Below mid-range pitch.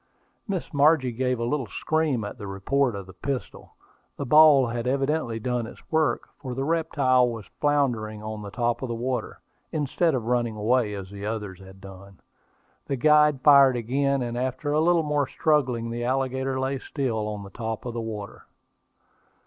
Yes: low, 125 Hz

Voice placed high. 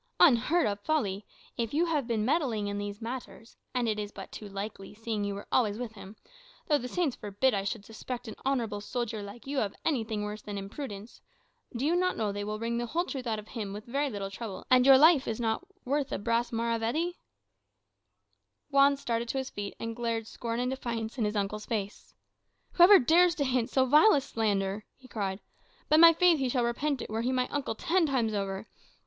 Yes: high, 235 Hz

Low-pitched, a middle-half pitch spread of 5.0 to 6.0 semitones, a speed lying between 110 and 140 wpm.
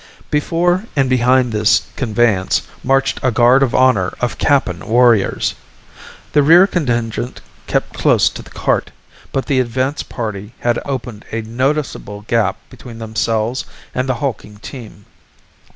No: low, 120 Hz; average, 3.3 semitones; slow, 135 wpm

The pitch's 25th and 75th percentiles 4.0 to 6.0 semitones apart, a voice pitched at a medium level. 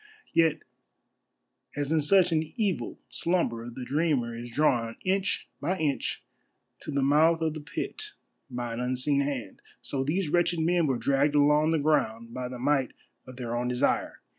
Yes: average, 4.6 semitones; medium, 145 Hz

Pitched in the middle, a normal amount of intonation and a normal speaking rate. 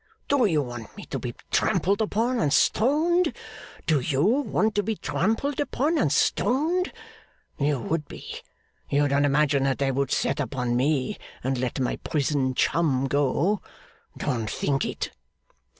No: medium, 150 Hz; wide, 8.6 semitones; average, 150 wpm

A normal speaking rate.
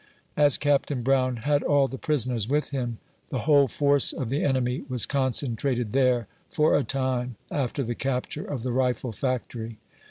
Yes: average, 165 wpm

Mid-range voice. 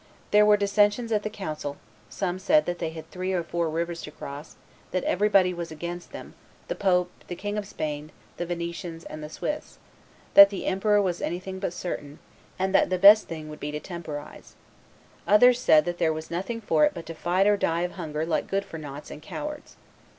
Yes: medium, 175 Hz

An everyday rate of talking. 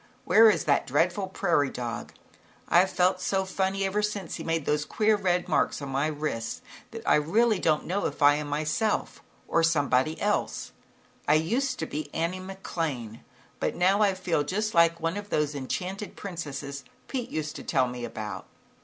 Yes: average, 180 wpm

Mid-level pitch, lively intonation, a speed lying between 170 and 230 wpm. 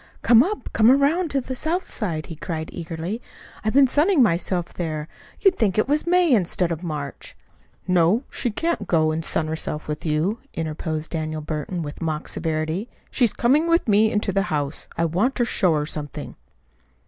Yes: medium, 180 Hz; wide, 7.7 semitones; average, 185 wpm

